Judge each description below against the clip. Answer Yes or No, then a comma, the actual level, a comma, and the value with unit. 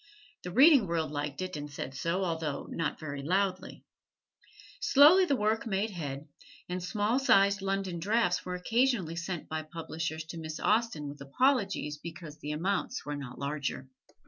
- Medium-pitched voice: Yes, medium, 175 Hz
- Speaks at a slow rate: No, average, 160 wpm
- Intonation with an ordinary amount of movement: Yes, average, 4.9 semitones